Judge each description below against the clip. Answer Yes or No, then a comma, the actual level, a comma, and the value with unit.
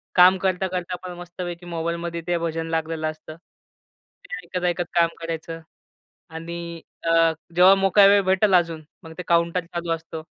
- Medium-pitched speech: Yes, medium, 170 Hz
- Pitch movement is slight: Yes, narrow, 1.5 semitones